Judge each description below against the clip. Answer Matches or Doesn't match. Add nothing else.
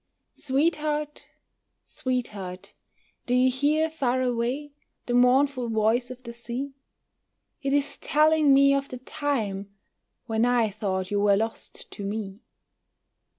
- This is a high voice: Matches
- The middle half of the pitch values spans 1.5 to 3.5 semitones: Doesn't match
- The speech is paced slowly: Matches